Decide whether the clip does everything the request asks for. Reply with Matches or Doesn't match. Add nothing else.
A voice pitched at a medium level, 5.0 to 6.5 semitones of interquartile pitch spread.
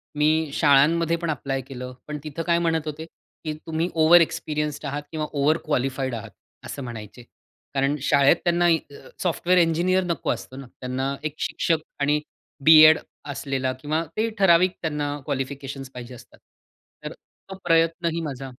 Doesn't match